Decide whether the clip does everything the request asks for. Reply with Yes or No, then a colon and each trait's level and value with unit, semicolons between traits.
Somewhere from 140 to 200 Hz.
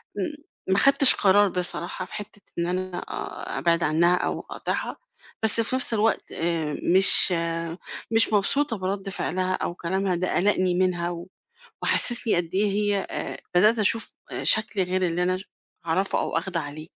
Yes: medium, 185 Hz